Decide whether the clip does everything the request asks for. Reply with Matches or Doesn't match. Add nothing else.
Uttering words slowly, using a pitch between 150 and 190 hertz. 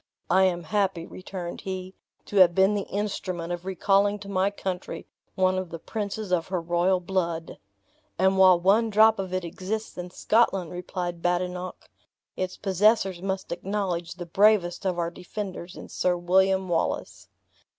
Doesn't match